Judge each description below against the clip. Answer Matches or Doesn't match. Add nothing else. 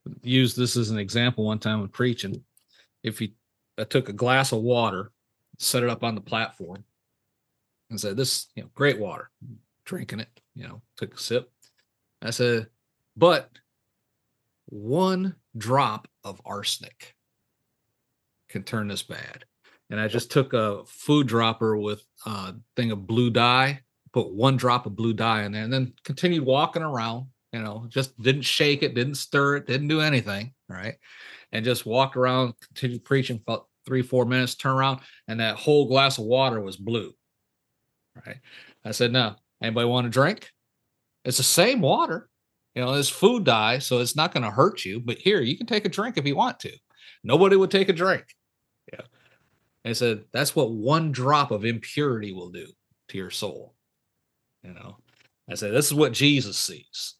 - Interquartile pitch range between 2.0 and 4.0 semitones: Matches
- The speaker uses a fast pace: Doesn't match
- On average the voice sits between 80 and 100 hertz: Doesn't match